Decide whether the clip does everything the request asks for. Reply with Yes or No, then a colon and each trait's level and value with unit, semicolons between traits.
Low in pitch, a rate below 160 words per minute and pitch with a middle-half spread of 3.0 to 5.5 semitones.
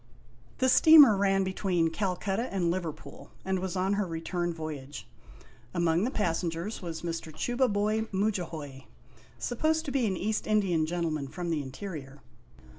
No: medium, 185 Hz; average, 145 wpm; average, 4.2 semitones